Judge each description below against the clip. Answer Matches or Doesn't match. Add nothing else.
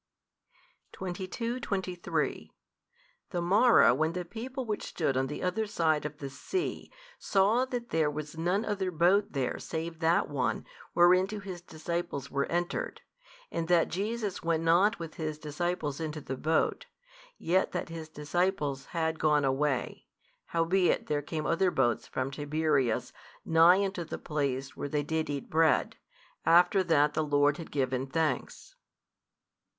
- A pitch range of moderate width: Matches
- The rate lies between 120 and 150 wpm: Matches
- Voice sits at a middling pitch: Matches